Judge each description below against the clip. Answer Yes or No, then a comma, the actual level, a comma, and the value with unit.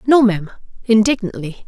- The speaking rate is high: No, slow, 105 wpm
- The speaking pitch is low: No, high, 215 Hz